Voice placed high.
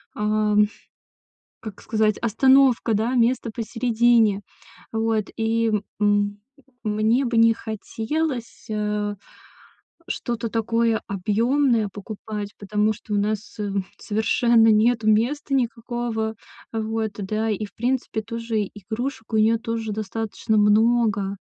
Yes: high, 220 Hz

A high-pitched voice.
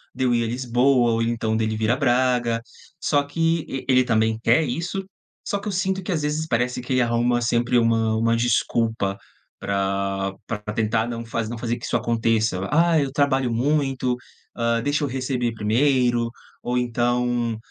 No: low, 120 Hz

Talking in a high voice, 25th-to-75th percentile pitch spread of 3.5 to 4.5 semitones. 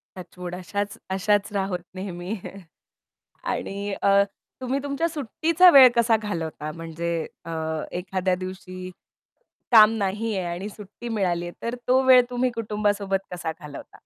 Yes: high, 195 Hz; average, 3.9 semitones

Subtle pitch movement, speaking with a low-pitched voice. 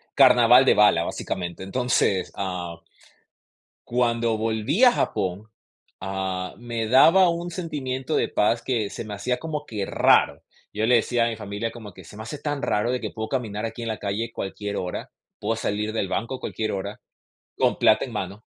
No: average, 3.6 semitones; low, 110 Hz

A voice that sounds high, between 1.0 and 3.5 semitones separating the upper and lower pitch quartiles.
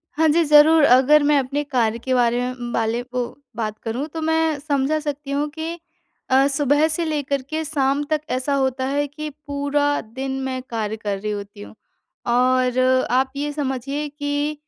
Yes: very high, 280 Hz; average, 2.8 semitones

